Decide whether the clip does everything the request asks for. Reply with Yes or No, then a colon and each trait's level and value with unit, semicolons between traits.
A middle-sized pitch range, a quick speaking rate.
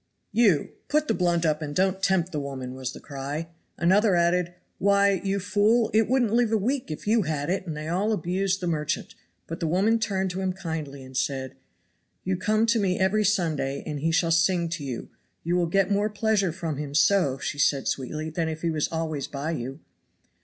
Yes: average, 4.7 semitones; fast, 215 wpm